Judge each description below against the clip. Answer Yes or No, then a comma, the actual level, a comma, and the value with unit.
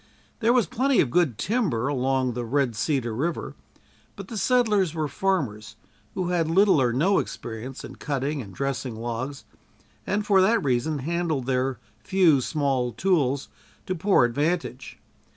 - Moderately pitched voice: Yes, medium, 145 Hz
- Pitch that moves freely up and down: Yes, wide, 6.7 semitones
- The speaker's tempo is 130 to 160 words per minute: Yes, average, 150 wpm